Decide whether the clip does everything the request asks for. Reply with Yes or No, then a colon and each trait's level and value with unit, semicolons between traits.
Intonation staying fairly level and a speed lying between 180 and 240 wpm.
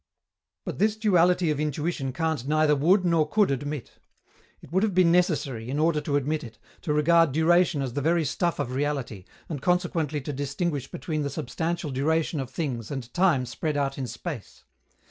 No: average, 3.7 semitones; average, 185 wpm